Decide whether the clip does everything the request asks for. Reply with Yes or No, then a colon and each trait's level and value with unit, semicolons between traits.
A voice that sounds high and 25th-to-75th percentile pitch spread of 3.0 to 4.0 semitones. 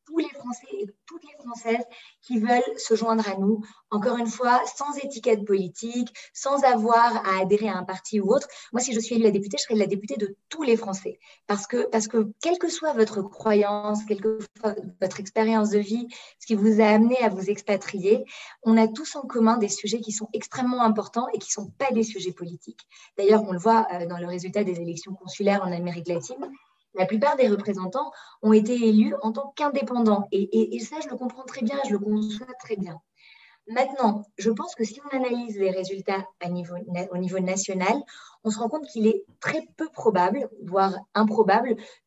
Yes: high, 220 Hz; average, 3.3 semitones